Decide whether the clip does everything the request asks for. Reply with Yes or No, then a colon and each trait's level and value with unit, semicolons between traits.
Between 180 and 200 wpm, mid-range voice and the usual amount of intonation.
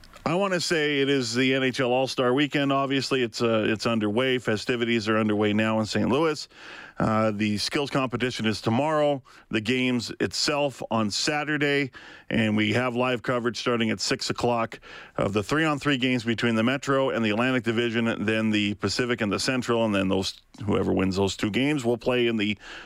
No: average, 195 wpm; low, 120 Hz; average, 3.4 semitones